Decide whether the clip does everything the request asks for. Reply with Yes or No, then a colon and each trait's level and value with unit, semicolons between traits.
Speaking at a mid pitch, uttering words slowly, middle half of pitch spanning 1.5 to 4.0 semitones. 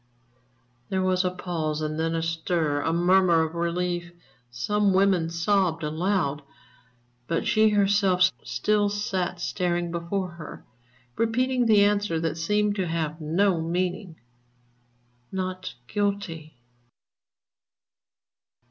Yes: medium, 180 Hz; slow, 115 wpm; average, 3.4 semitones